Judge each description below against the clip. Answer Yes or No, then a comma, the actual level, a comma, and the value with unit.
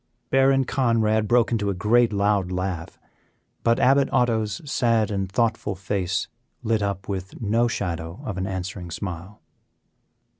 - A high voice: No, low, 105 Hz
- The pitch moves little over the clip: No, average, 3.5 semitones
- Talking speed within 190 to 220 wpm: No, average, 140 wpm